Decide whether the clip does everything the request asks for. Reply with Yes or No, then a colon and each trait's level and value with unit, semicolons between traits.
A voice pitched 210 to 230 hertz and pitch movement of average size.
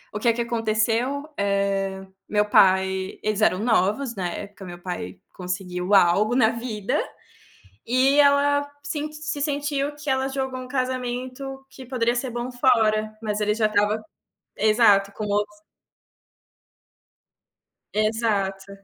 Yes: high, 220 Hz; average, 4.5 semitones